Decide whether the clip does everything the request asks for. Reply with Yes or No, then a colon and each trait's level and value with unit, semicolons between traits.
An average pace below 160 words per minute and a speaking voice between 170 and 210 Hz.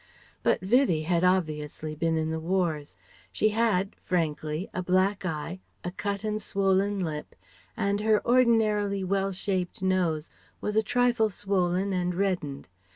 Yes: average, 145 wpm; medium, 185 Hz